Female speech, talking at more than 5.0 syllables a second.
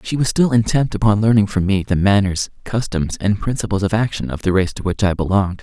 No: male; 5.9 syllables/s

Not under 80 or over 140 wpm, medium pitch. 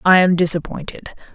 Yes: slow, 135 wpm; medium, 175 Hz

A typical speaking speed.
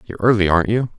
No: fast, 245 wpm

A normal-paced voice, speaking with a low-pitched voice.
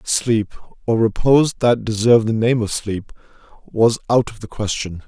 Yes: average, 165 wpm; low, 115 Hz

